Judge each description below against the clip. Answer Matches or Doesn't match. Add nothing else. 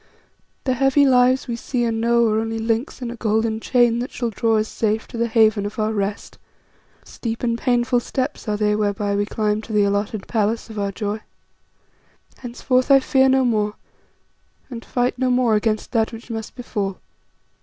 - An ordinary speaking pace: Matches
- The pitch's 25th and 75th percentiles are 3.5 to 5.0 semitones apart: Doesn't match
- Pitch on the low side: Doesn't match